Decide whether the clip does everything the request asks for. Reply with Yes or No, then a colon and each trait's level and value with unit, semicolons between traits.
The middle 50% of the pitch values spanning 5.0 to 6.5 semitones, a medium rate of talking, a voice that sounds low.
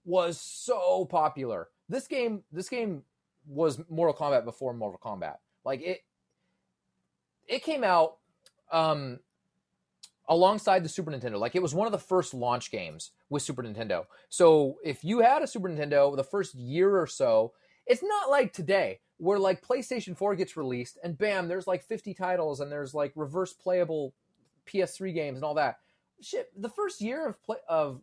No: wide, 5.5 semitones; average, 170 wpm; medium, 180 Hz